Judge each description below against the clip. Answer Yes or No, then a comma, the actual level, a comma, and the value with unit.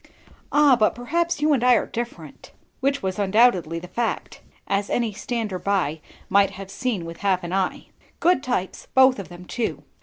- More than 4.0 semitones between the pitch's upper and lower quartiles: Yes, average, 5.1 semitones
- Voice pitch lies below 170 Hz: No, high, 210 Hz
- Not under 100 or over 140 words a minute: No, average, 180 wpm